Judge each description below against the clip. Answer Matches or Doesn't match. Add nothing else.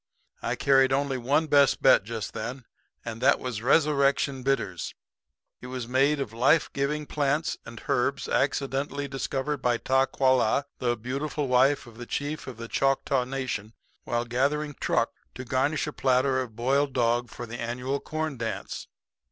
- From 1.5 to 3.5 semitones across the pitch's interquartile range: Matches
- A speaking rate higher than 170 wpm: Doesn't match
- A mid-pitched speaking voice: Doesn't match